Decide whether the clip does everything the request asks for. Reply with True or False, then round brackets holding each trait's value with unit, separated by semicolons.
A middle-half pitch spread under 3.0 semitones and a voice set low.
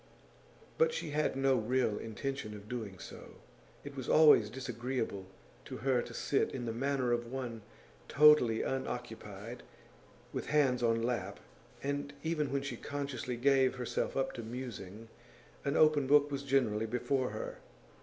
False (3.3 semitones; 125 Hz)